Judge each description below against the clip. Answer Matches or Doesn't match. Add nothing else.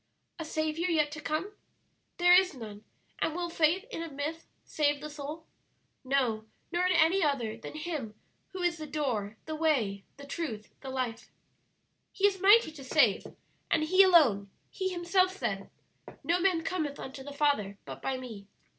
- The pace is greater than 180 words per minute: Doesn't match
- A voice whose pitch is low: Doesn't match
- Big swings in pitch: Doesn't match